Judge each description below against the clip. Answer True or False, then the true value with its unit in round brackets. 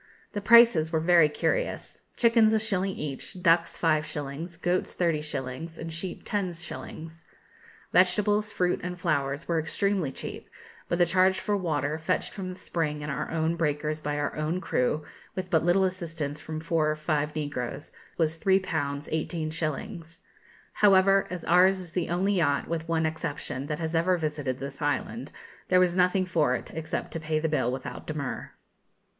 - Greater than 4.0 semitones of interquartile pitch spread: False (3.2 semitones)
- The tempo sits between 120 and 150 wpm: False (170 wpm)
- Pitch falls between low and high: True (165 Hz)